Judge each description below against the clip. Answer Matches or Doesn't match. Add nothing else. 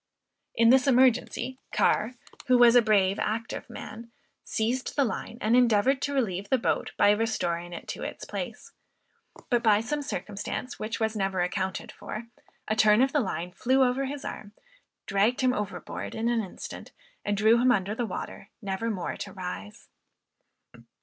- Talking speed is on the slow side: Doesn't match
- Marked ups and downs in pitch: Doesn't match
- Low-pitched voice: Doesn't match